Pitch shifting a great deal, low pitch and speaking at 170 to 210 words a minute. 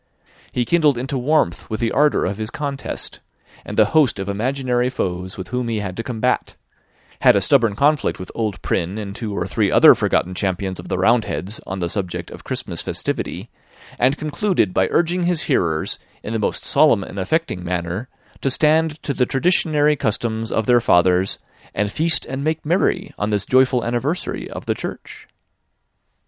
Yes: wide, 6.8 semitones; low, 120 Hz; average, 185 wpm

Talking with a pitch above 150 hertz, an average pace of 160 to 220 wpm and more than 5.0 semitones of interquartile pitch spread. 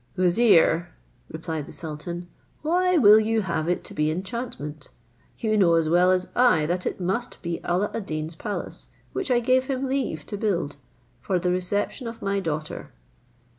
Yes: medium, 185 Hz; average, 170 wpm; wide, 5.6 semitones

